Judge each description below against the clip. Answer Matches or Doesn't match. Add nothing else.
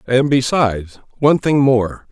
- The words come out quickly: Doesn't match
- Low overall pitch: Matches